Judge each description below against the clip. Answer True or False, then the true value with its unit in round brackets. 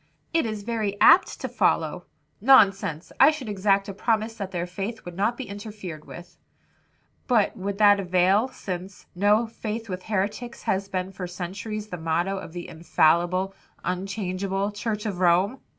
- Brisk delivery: False (160 wpm)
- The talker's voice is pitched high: True (195 Hz)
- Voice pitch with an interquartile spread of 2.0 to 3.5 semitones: True (2.9 semitones)